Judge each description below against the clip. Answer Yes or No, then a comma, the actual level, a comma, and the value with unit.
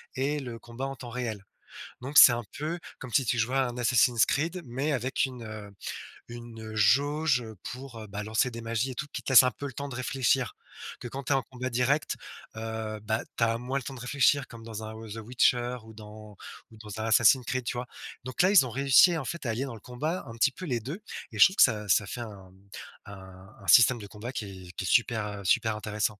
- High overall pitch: No, low, 120 Hz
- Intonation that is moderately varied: Yes, average, 3.3 semitones